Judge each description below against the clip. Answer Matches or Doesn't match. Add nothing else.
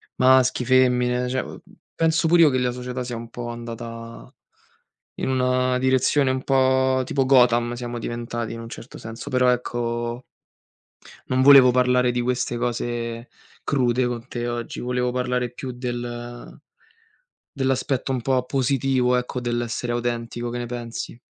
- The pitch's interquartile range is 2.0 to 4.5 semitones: Doesn't match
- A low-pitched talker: Matches